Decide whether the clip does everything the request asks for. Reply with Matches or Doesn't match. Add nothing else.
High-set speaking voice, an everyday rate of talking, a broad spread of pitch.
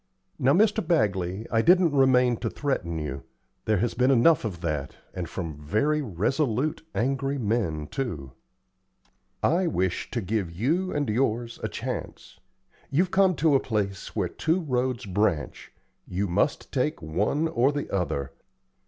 Doesn't match